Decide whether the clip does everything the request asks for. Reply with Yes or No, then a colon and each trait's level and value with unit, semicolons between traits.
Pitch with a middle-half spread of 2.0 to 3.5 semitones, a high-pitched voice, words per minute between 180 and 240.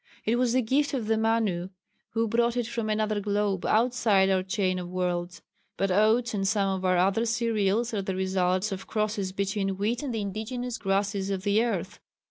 Yes: average, 3.0 semitones; high, 205 Hz; average, 195 wpm